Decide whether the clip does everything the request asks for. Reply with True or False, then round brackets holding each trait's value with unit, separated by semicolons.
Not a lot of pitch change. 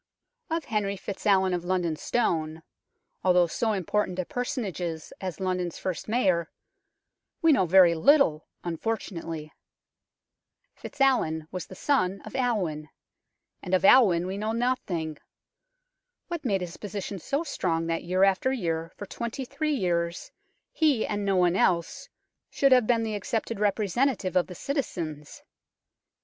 False (5.3 semitones)